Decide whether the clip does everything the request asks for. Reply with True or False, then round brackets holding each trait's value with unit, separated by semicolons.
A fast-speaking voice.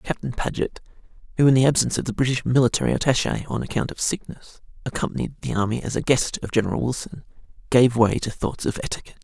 False (195 wpm)